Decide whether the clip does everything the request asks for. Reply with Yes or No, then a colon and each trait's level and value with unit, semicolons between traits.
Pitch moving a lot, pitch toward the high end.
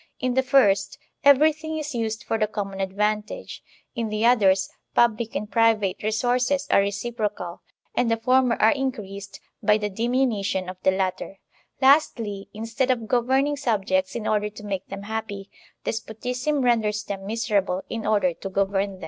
No: average, 3.7 semitones; high, 215 Hz